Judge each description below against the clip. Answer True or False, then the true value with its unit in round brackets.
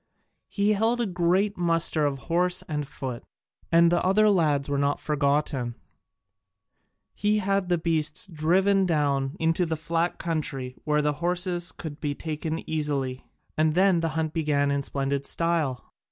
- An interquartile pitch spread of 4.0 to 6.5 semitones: False (3.6 semitones)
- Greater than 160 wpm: False (155 wpm)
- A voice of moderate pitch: True (160 Hz)